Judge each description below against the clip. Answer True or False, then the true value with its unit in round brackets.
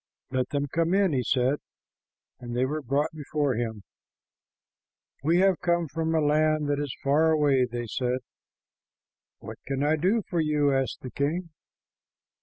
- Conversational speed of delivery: True (160 wpm)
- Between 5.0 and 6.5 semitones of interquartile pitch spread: False (3.5 semitones)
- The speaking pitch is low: False (145 Hz)